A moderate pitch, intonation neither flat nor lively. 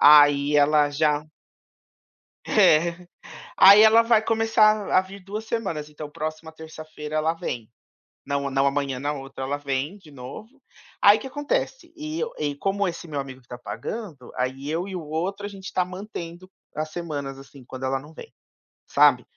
No: medium, 155 Hz; wide, 5.8 semitones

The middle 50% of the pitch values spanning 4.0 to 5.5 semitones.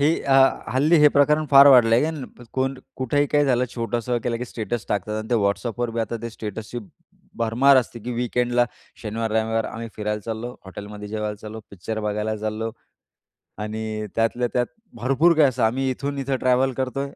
No: average, 3.3 semitones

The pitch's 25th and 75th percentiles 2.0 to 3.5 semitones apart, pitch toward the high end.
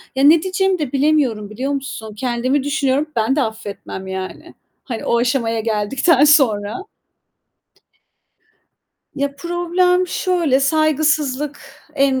No: average, 4.8 semitones; very high, 275 Hz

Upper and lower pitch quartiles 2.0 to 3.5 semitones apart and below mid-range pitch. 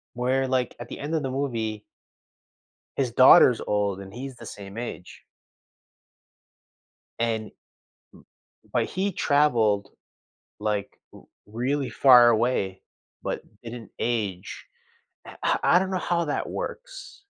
No: average, 4.3 semitones; low, 120 Hz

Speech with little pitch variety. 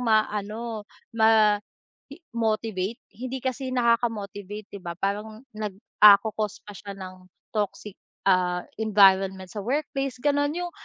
No: average, 3.0 semitones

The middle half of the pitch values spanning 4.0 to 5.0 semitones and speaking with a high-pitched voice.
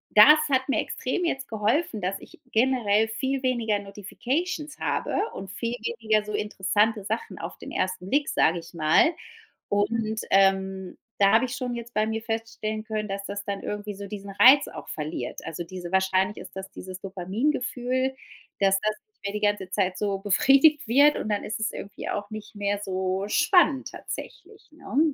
Yes: average, 4.5 semitones; high, 210 Hz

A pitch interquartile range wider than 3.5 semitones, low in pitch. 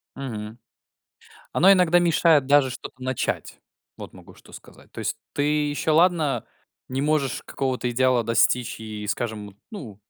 Yes: average, 4.9 semitones; low, 130 Hz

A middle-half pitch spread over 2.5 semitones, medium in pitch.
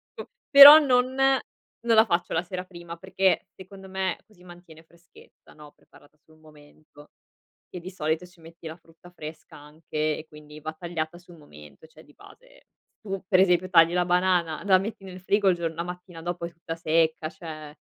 Yes: average, 2.9 semitones; medium, 170 Hz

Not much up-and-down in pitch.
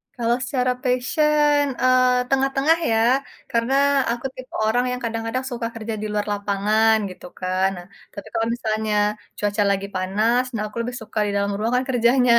No: average, 3.2 semitones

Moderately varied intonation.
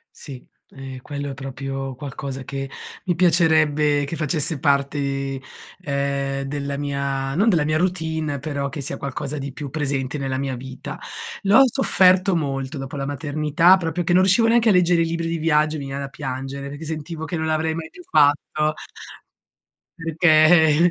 Yes: average, 3.0 semitones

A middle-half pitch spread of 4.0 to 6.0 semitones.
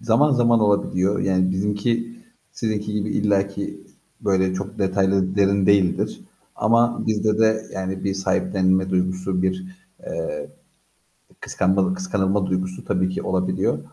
No: narrow, 2.6 semitones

